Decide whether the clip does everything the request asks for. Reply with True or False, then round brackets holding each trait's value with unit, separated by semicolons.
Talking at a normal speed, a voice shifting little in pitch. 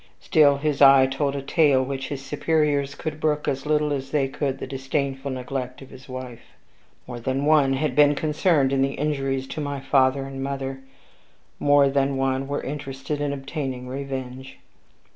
True (175 wpm; 1.4 semitones)